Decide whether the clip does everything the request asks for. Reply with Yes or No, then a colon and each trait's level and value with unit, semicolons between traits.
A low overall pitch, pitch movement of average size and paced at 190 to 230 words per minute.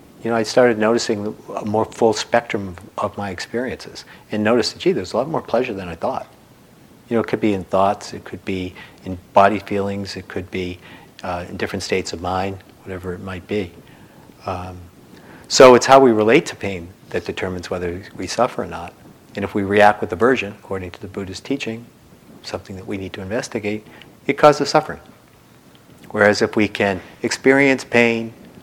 Yes: low, 100 Hz; average, 3.6 semitones; average, 195 wpm